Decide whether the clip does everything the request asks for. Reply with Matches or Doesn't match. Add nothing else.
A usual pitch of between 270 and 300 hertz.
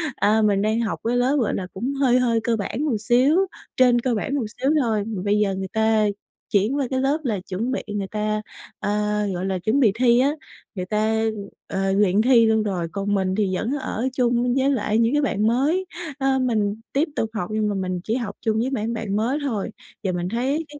Doesn't match